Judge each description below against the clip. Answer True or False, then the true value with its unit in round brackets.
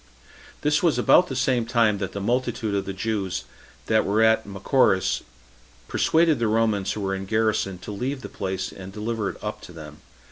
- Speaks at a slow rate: False (190 wpm)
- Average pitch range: True (3.5 semitones)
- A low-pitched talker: True (110 Hz)